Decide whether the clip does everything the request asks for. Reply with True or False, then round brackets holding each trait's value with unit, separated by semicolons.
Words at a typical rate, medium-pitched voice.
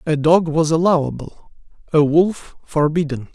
False (125 wpm; 160 Hz)